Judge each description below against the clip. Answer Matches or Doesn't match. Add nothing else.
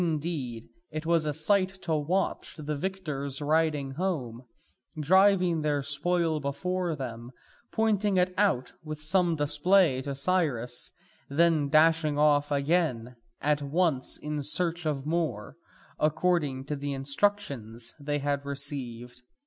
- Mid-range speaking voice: Matches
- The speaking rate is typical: Doesn't match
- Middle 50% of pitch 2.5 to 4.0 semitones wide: Matches